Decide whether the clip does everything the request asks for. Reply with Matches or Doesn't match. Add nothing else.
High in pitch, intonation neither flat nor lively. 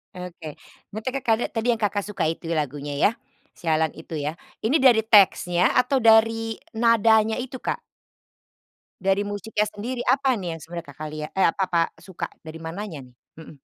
Doesn't match